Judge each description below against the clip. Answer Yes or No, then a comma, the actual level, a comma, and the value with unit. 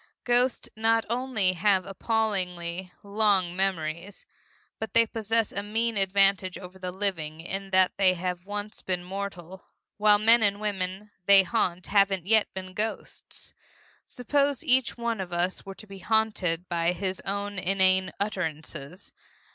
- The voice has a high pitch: Yes, high, 195 Hz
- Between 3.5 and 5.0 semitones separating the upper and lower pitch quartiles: No, average, 2.7 semitones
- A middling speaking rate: Yes, average, 145 wpm